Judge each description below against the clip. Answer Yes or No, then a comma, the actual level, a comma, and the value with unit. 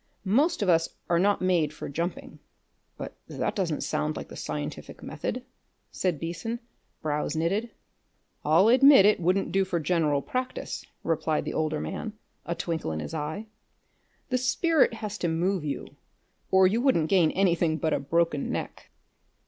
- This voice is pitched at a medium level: Yes, medium, 170 Hz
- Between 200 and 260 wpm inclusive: No, average, 160 wpm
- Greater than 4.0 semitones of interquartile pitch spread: Yes, average, 4.5 semitones